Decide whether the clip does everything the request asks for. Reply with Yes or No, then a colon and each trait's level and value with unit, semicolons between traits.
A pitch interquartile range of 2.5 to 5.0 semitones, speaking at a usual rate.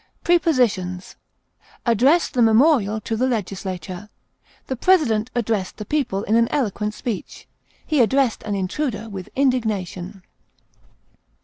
No: average, 4.6 semitones; slow, 115 wpm